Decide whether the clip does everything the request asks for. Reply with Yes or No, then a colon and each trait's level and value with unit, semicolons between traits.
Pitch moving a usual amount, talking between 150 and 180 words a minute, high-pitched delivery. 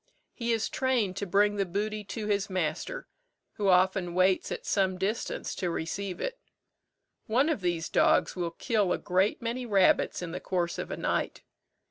Yes: average, 3.1 semitones; average, 175 wpm; high, 195 Hz